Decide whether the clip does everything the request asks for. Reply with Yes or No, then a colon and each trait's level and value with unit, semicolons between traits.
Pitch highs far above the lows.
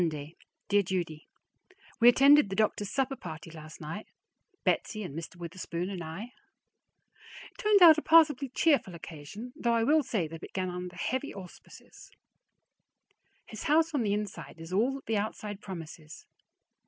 Yes: wide, 6.9 semitones